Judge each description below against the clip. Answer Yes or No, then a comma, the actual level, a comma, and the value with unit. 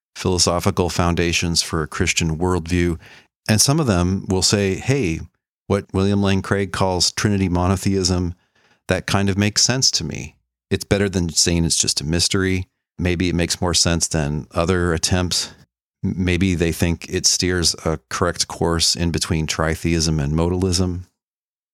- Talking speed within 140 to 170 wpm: Yes, average, 155 wpm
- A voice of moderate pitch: No, very low, 90 Hz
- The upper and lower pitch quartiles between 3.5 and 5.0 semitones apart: No, average, 2.7 semitones